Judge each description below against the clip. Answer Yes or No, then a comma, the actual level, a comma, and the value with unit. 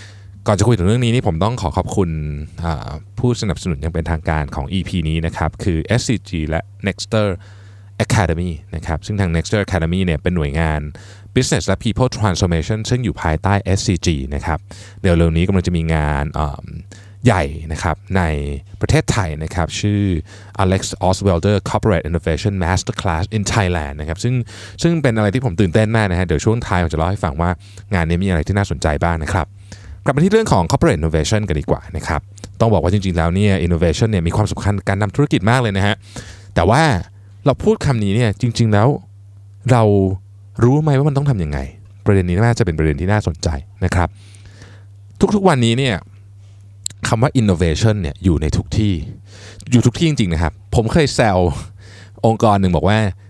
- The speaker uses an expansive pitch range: No, average, 4.1 semitones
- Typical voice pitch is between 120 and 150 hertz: No, low, 100 Hz